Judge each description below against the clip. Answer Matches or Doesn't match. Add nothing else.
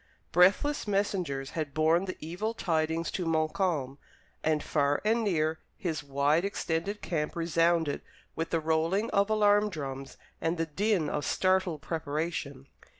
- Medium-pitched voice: Matches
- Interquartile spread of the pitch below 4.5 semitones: Matches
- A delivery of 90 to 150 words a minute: Matches